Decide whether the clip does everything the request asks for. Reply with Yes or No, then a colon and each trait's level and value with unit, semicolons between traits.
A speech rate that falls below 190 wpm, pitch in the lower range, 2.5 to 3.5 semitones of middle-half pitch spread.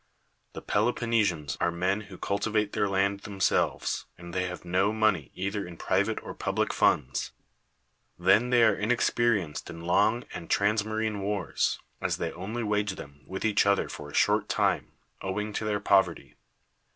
Yes: average, 160 wpm; low, 100 Hz; average, 2.8 semitones